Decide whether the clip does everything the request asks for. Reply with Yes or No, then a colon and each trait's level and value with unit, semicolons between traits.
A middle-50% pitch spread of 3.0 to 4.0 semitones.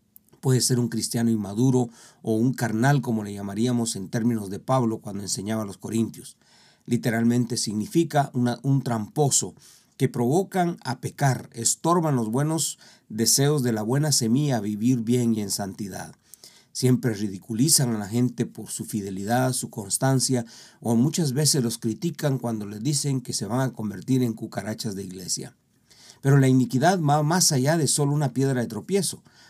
Yes: average, 3.4 semitones